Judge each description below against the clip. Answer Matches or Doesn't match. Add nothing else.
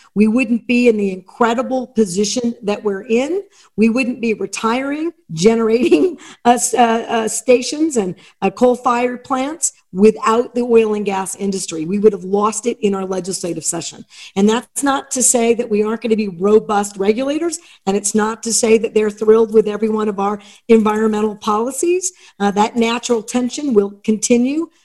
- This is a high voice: Matches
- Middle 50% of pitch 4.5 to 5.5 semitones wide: Doesn't match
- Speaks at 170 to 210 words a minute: Matches